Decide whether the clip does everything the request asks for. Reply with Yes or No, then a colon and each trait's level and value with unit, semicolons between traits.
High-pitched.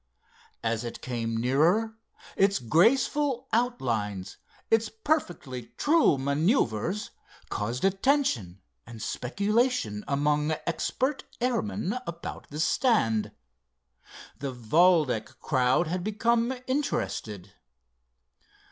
No: medium, 165 Hz